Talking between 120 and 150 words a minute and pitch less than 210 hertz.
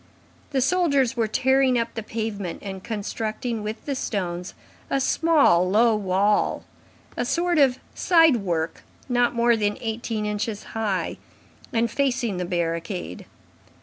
No: slow, 135 wpm; high, 225 Hz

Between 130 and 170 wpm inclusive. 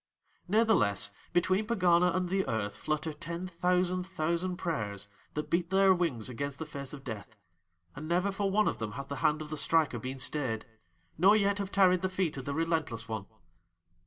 No: average, 190 wpm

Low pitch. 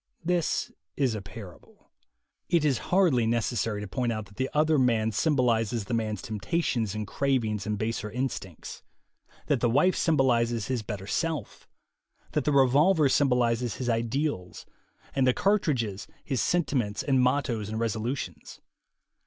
Yes: low, 120 Hz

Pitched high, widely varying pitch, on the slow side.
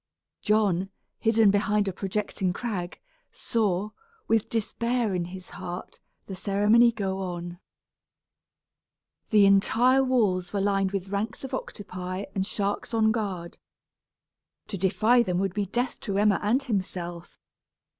No: high, 200 Hz; average, 3.0 semitones; slow, 130 wpm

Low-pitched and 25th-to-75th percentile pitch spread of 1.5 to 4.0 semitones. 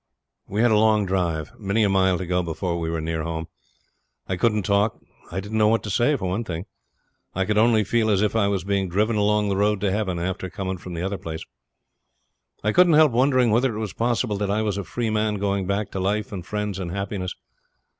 Yes: low, 100 Hz; narrow, 2.6 semitones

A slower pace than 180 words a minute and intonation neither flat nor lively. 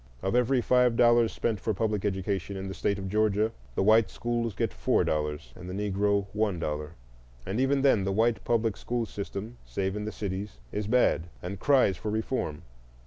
No: average, 195 wpm; average, 3.3 semitones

